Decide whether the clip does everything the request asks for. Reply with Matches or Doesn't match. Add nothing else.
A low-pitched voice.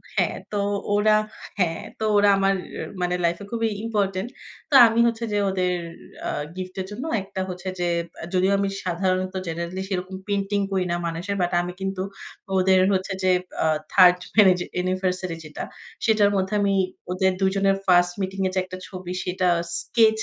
Doesn't match